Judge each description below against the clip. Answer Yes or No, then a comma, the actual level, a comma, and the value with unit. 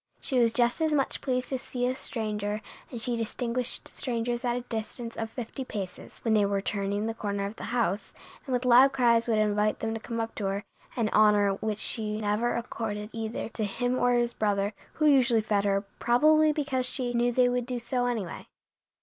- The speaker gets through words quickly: Yes, fast, 210 wpm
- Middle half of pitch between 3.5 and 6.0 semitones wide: No, average, 2.7 semitones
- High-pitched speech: Yes, high, 230 Hz